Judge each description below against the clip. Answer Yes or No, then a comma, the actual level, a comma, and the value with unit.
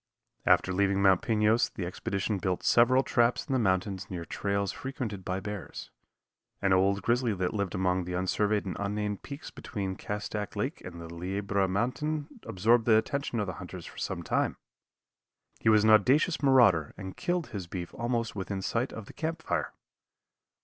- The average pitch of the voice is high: No, low, 100 Hz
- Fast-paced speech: No, average, 175 wpm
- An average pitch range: Yes, average, 3.9 semitones